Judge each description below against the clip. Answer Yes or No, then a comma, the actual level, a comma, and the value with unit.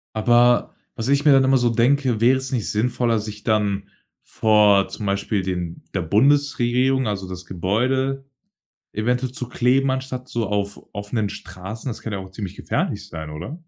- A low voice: Yes, low, 115 Hz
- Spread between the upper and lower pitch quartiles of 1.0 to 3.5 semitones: No, average, 4.5 semitones